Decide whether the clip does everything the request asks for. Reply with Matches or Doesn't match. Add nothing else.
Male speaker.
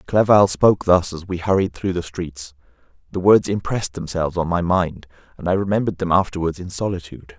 Matches